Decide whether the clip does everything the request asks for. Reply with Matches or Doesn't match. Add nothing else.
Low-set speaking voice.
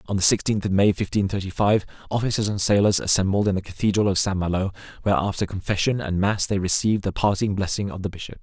Matches